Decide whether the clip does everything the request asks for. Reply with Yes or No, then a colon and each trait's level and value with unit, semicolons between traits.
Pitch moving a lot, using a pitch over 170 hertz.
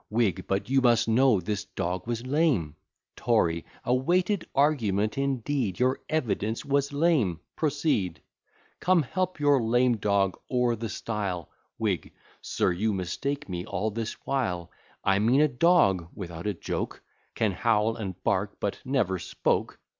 No: wide, 6.0 semitones; low, 115 Hz